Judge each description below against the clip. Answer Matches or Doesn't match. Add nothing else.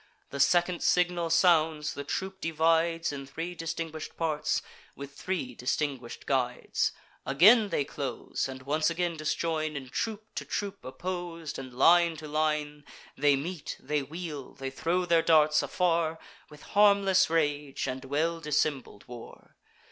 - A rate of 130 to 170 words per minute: Matches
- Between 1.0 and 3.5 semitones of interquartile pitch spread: Matches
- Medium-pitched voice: Matches